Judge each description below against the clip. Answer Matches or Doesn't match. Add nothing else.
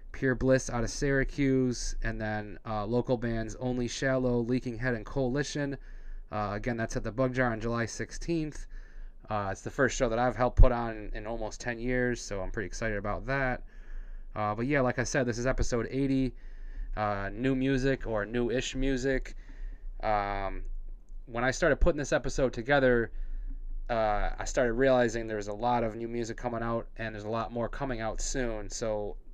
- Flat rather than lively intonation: Doesn't match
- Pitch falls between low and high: Doesn't match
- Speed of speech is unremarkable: Matches